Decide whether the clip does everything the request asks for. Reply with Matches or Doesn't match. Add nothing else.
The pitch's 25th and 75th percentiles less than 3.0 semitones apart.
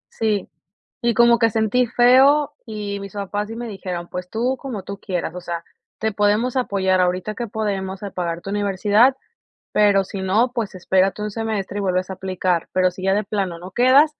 Doesn't match